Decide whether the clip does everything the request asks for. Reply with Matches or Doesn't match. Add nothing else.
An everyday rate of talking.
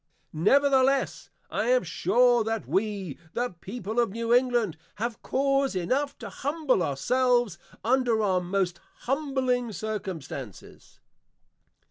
Doesn't match